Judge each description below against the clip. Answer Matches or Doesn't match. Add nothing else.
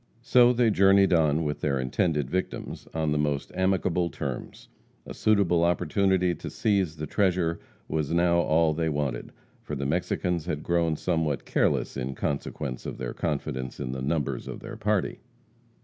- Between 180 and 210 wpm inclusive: Doesn't match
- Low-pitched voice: Matches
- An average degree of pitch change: Matches